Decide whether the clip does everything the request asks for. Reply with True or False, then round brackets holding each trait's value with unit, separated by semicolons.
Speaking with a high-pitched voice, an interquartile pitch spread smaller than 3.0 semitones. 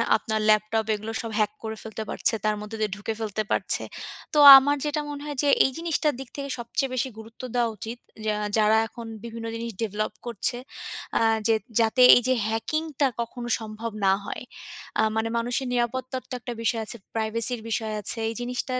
True (230 Hz; 2.6 semitones)